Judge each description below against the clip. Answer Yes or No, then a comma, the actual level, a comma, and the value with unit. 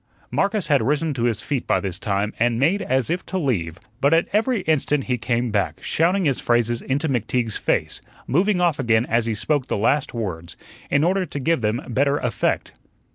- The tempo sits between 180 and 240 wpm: Yes, average, 200 wpm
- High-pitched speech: No, low, 130 Hz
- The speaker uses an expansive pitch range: Yes, wide, 5.7 semitones